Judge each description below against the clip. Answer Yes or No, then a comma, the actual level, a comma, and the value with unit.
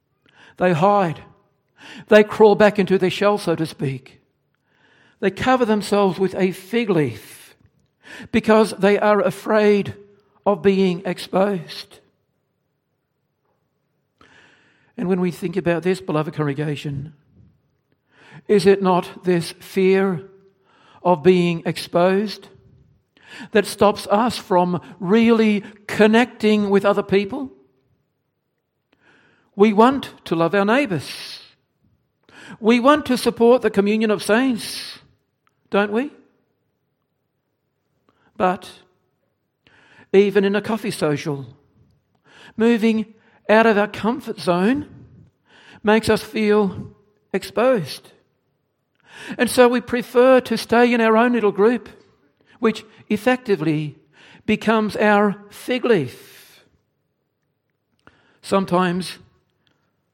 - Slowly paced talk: Yes, slow, 100 wpm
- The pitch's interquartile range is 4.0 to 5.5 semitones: No, average, 3.4 semitones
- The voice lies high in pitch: Yes, high, 200 Hz